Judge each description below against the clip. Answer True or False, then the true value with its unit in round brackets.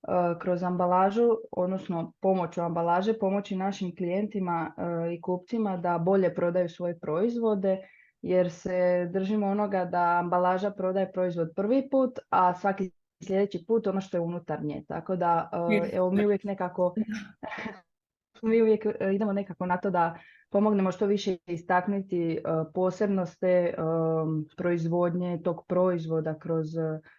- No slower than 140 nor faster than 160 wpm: False (125 wpm)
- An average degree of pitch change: False (2.3 semitones)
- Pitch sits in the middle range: True (180 Hz)